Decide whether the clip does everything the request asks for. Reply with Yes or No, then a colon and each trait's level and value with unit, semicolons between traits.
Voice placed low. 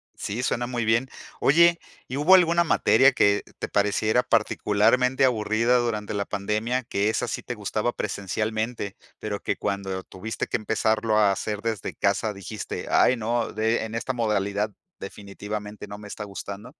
Yes: low, 110 Hz